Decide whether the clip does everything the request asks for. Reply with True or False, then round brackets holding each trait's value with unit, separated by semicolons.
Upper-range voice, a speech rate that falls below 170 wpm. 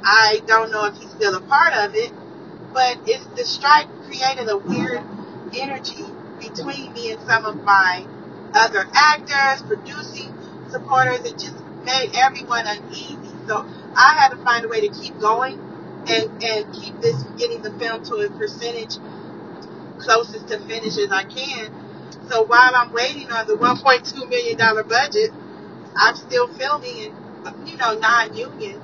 True (250 Hz; 155 wpm)